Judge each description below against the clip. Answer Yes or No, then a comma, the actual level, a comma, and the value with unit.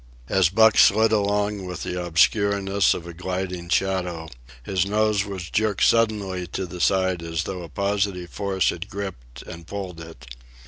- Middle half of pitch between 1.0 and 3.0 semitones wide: Yes, narrow, 2.6 semitones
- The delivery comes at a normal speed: Yes, average, 165 wpm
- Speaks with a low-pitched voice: Yes, very low, 95 Hz